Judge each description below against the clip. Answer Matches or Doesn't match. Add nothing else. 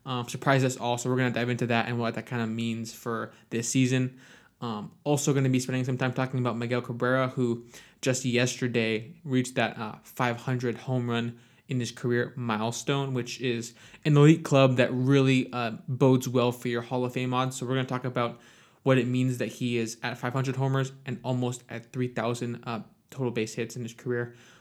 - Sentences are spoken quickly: Matches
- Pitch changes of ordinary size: Doesn't match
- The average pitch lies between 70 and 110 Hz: Doesn't match